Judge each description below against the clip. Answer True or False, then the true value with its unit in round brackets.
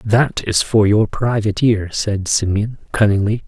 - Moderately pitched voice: False (105 Hz)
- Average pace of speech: True (155 wpm)